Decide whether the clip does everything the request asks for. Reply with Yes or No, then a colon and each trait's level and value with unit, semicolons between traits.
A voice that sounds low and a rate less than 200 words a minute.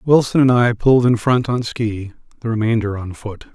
No: low, 115 Hz; fast, 205 wpm